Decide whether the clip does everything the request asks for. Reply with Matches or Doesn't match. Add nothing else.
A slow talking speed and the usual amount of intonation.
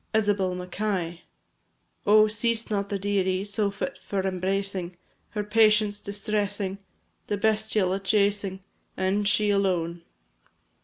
Doesn't match